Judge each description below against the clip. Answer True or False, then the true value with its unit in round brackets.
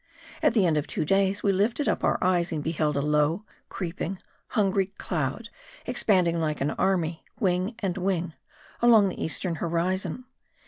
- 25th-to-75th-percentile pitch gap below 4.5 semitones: True (3.4 semitones)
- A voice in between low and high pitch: True (180 Hz)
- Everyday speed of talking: True (165 wpm)